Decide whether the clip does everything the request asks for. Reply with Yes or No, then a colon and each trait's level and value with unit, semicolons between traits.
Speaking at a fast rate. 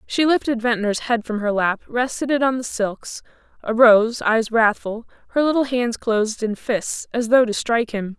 No: average, 190 wpm